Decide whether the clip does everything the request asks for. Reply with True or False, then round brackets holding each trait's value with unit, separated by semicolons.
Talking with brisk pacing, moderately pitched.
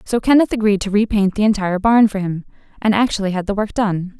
False (230 wpm; 205 Hz)